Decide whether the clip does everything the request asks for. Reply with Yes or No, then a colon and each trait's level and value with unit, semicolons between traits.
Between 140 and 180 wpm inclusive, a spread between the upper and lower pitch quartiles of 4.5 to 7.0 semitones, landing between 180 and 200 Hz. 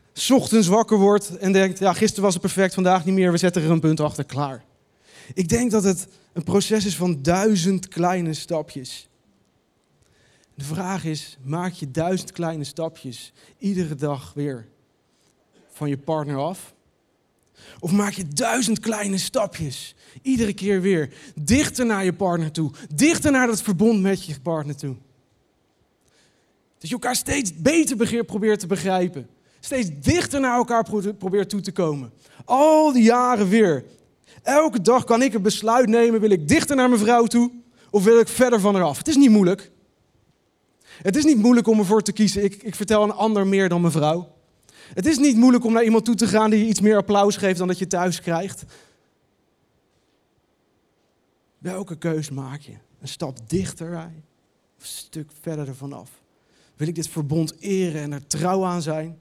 Yes: average, 175 wpm; wide, 5.5 semitones; high, 190 Hz